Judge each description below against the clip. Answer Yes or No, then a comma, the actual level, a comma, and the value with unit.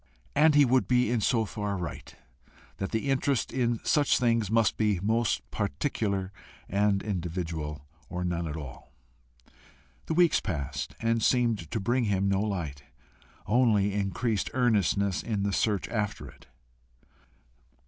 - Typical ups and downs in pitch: Yes, average, 3.9 semitones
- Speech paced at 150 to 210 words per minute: No, average, 140 wpm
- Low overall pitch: Yes, low, 105 Hz